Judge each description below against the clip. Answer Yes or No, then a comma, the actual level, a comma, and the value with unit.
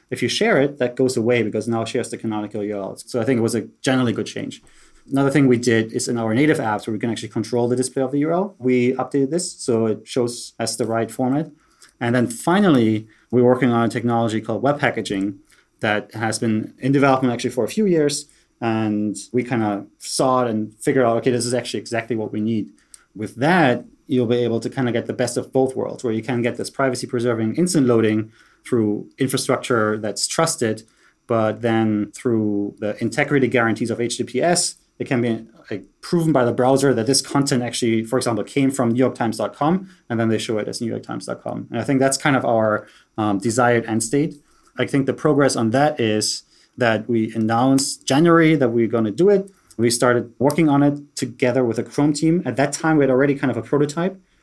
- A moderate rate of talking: No, fast, 220 wpm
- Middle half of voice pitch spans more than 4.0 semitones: No, average, 3.2 semitones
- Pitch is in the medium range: No, low, 120 Hz